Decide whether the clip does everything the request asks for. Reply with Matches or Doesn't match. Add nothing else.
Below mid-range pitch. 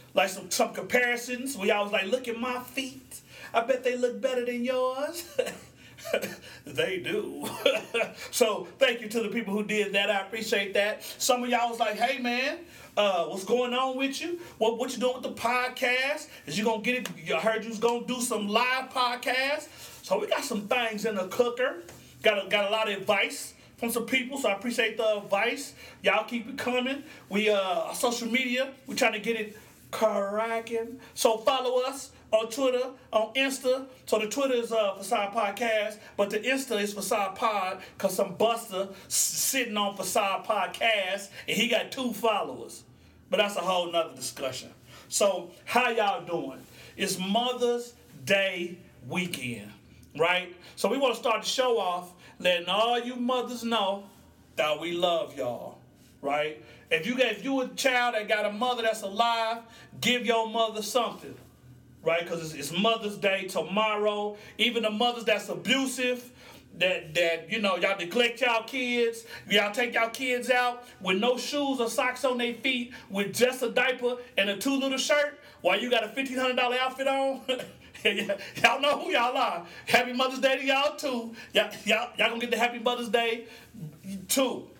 Doesn't match